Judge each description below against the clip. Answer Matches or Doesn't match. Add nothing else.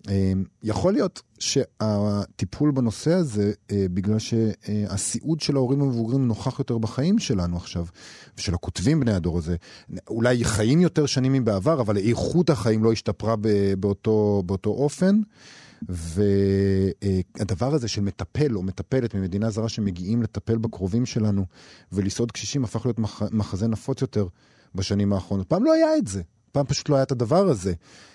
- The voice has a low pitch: Matches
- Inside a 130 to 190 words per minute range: Matches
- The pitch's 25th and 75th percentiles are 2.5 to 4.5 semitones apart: Doesn't match